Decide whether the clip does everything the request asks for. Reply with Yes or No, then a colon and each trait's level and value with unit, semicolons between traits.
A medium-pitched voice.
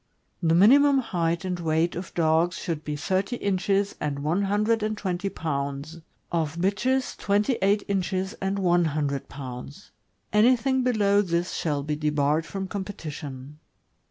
Yes: medium, 180 Hz